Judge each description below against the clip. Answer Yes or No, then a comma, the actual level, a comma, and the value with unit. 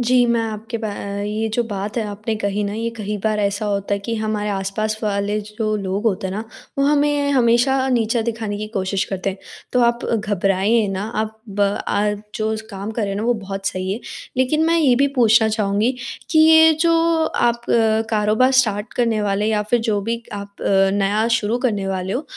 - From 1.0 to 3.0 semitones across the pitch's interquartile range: Yes, average, 2.7 semitones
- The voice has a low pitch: No, high, 215 Hz